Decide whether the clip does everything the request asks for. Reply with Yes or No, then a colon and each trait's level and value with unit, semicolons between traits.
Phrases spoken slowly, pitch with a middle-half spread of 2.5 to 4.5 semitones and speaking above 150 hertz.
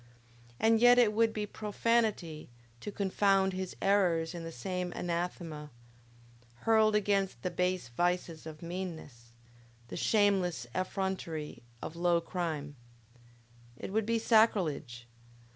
Yes: slow, 120 wpm; average, 3.9 semitones; medium, 185 Hz